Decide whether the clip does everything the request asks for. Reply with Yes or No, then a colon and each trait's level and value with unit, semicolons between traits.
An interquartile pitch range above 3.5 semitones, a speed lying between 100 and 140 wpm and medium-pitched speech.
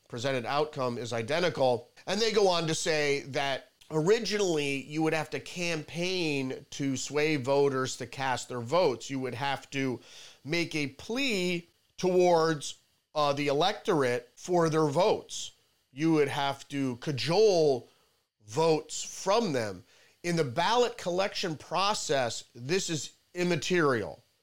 Yes: average, 4.4 semitones; slow, 135 wpm; medium, 150 Hz